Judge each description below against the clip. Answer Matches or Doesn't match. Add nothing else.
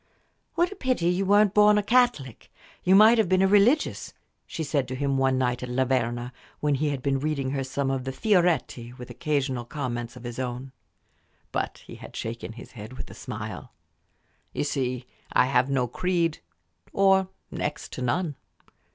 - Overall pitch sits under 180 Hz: Matches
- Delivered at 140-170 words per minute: Doesn't match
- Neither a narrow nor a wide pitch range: Doesn't match